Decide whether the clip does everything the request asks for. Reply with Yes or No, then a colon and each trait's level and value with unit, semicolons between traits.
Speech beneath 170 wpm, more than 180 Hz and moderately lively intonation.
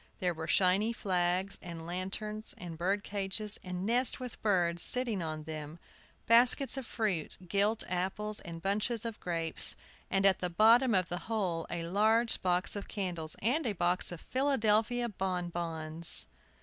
Yes: average, 150 wpm; high, 190 Hz; average, 4.0 semitones